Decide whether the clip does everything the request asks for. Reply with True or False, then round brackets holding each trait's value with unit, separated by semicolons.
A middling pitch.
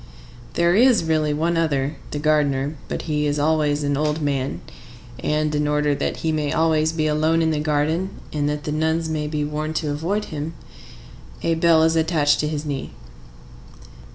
True (155 Hz)